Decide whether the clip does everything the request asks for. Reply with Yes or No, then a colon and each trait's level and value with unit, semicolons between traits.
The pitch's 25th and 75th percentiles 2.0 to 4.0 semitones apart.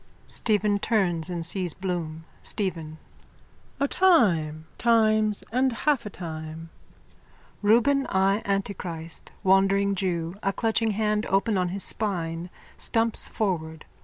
No: average, 4.4 semitones